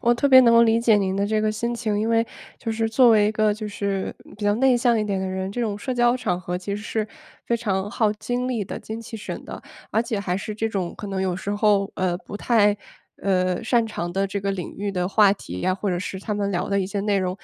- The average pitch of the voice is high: Yes, high, 210 Hz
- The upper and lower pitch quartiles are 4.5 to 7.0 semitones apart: No, average, 2.7 semitones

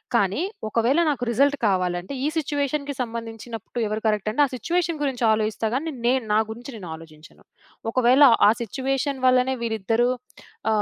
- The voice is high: Yes, high, 240 Hz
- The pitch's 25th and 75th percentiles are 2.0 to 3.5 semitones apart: No, average, 4.1 semitones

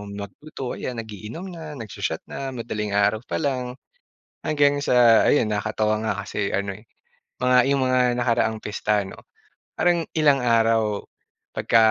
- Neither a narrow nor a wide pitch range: Yes, average, 4.4 semitones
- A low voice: Yes, low, 115 Hz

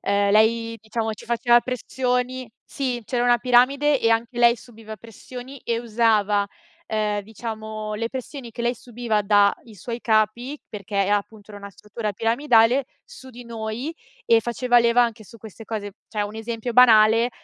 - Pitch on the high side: Yes, high, 230 Hz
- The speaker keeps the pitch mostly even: Yes, narrow, 2.1 semitones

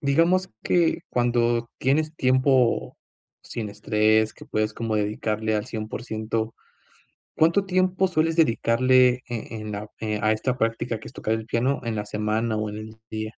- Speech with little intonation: No, average, 3.3 semitones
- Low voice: Yes, low, 115 Hz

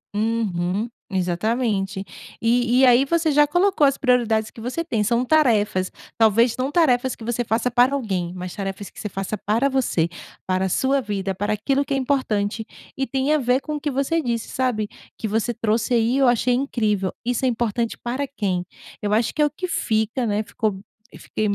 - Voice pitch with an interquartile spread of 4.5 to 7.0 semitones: No, average, 4.0 semitones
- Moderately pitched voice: No, high, 235 Hz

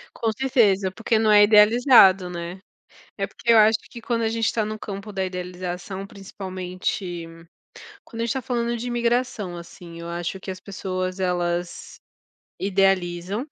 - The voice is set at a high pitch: Yes, high, 195 Hz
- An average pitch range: Yes, average, 3.7 semitones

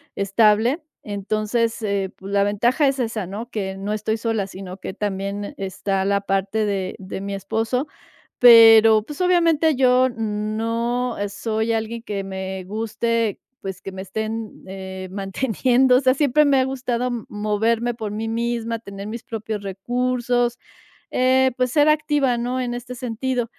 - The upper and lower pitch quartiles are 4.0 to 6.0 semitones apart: No, average, 3.6 semitones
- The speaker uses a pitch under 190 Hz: No, high, 225 Hz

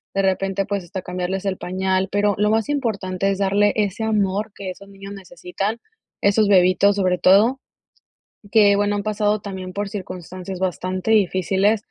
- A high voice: Yes, high, 195 Hz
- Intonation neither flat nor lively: No, narrow, 1.8 semitones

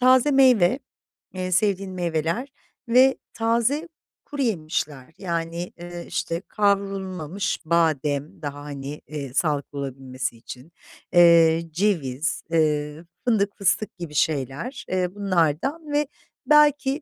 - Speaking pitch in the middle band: Yes, medium, 175 Hz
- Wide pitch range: Yes, wide, 6.2 semitones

